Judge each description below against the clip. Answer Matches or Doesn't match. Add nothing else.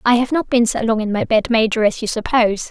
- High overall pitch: Matches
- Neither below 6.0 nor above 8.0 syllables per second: Matches